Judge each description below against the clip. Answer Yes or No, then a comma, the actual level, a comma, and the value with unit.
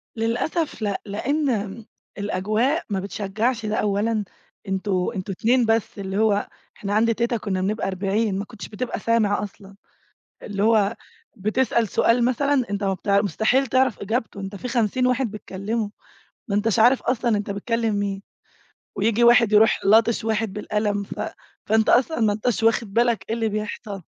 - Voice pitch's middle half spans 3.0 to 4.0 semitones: No, narrow, 2.5 semitones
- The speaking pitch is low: No, high, 215 Hz